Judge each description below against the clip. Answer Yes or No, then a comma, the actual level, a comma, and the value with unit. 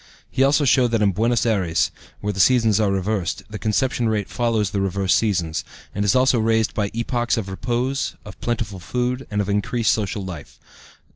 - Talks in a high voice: No, low, 110 Hz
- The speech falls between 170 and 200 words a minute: Yes, average, 190 wpm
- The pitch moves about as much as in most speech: Yes, average, 3.4 semitones